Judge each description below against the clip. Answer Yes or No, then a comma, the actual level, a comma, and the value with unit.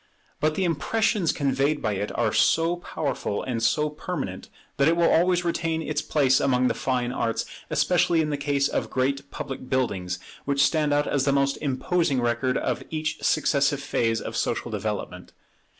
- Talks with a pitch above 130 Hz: Yes, medium, 140 Hz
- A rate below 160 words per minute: No, average, 175 wpm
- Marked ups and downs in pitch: No, average, 3.6 semitones